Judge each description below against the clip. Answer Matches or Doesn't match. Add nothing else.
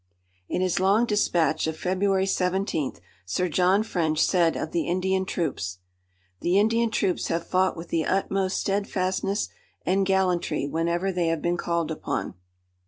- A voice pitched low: Doesn't match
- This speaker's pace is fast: Doesn't match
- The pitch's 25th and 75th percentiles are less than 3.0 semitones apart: Matches